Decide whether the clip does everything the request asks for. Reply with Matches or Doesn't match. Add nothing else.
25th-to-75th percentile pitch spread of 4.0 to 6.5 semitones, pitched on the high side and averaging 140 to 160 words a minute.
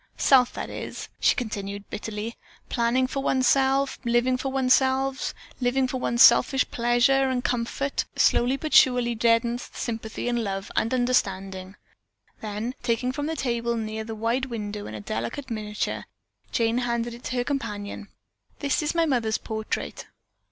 Doesn't match